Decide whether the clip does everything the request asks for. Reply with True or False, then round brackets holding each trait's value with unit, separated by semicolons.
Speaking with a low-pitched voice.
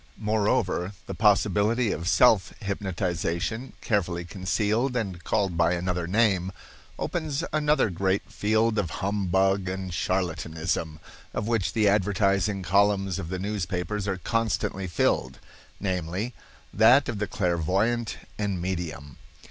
True (95 Hz)